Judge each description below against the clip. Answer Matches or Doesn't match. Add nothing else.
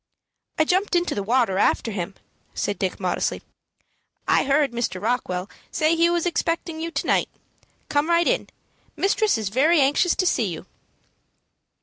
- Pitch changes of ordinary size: Doesn't match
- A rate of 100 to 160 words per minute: Matches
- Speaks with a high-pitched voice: Matches